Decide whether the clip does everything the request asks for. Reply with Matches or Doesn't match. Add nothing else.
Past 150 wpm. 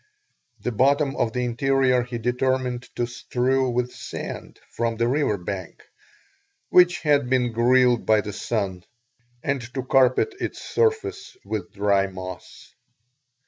Doesn't match